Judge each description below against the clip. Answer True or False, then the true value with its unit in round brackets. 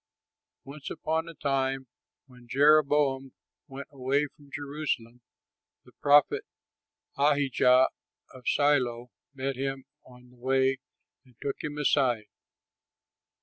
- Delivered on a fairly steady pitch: True (2.1 semitones)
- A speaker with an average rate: False (105 wpm)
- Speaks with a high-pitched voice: False (135 Hz)